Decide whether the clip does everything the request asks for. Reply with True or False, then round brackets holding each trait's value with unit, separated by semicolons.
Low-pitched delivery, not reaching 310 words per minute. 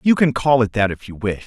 False (120 Hz; 325 wpm)